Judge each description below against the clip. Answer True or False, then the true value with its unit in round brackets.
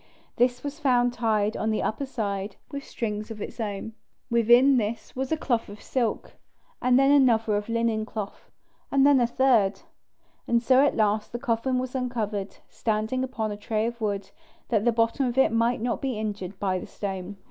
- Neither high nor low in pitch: False (230 Hz)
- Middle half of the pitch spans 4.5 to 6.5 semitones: False (3.1 semitones)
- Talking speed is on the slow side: False (190 wpm)